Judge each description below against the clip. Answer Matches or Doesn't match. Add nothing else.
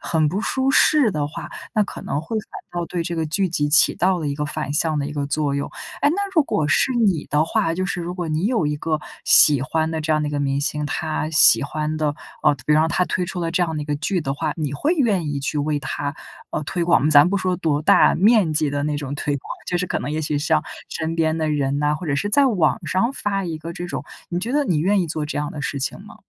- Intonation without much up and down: Doesn't match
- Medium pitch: Matches